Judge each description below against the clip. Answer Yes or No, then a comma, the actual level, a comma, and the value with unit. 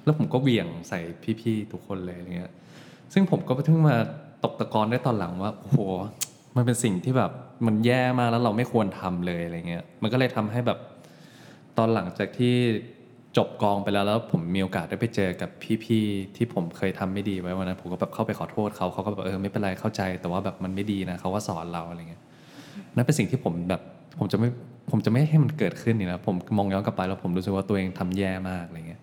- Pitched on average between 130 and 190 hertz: No, low, 100 Hz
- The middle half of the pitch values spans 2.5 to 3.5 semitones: No, average, 4.1 semitones